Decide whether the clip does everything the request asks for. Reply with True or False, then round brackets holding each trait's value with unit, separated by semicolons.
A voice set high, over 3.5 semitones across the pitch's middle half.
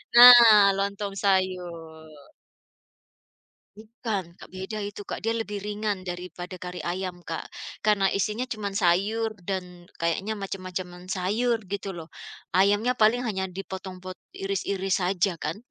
False (195 Hz; 2.5 semitones)